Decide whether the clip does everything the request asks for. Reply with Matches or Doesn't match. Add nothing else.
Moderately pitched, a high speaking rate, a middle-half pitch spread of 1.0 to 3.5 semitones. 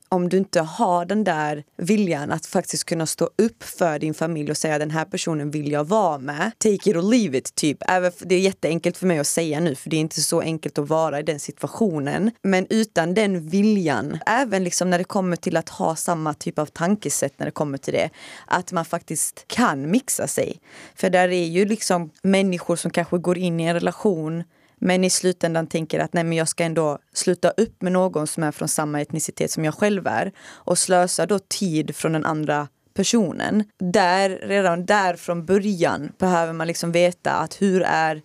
Matches